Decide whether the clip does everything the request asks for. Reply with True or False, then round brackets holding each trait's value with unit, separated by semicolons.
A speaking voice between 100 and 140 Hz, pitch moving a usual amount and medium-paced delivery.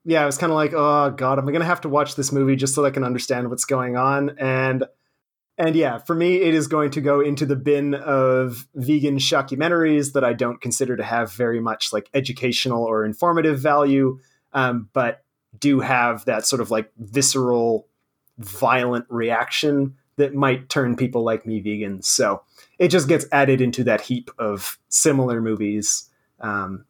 True (135 Hz; 3.2 semitones; 185 wpm)